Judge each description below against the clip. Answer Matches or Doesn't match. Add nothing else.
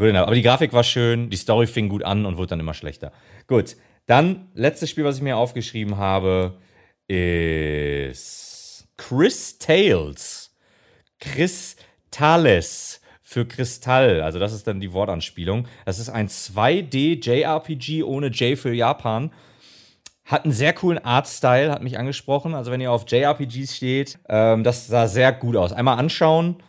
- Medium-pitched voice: Doesn't match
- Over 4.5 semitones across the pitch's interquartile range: Matches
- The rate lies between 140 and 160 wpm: Matches